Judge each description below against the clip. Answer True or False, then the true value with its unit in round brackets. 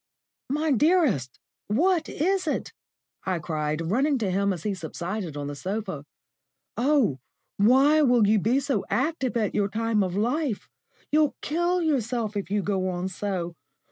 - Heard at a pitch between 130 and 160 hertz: False (215 Hz)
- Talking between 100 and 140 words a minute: False (155 wpm)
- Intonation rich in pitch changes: True (7.2 semitones)